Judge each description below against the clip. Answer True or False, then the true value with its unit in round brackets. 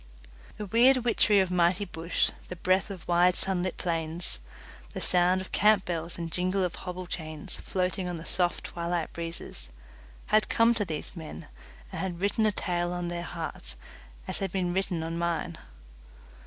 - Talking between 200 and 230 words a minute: False (170 wpm)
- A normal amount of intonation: False (2.1 semitones)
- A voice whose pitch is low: False (180 Hz)